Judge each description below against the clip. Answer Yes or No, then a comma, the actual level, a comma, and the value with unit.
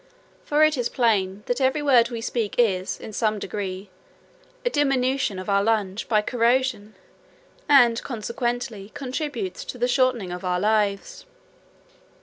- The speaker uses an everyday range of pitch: Yes, average, 4.1 semitones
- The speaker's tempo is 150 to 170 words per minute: No, average, 140 wpm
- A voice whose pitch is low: No, high, 230 Hz